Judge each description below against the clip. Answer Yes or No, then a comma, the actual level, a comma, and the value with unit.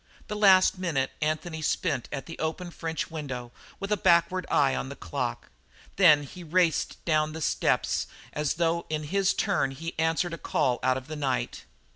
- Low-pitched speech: No, medium, 160 Hz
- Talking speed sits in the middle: Yes, average, 180 wpm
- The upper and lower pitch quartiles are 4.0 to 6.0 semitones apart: No, average, 3.3 semitones